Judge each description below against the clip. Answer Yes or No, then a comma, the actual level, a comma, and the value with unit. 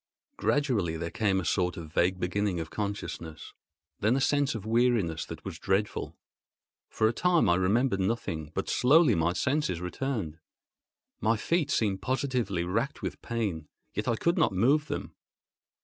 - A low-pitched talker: Yes, low, 105 Hz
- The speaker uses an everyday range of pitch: No, wide, 6.1 semitones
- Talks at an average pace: Yes, average, 160 wpm